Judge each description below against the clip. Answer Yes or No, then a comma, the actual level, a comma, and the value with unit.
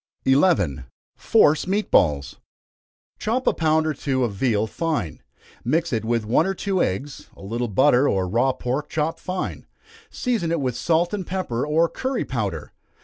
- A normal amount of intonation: No, wide, 6.6 semitones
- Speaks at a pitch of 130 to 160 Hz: Yes, medium, 140 Hz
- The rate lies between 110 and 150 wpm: No, average, 165 wpm